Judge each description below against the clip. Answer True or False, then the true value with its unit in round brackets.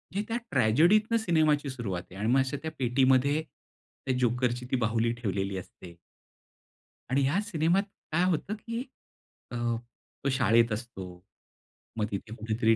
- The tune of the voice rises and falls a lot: True (5.8 semitones)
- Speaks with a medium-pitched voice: False (130 Hz)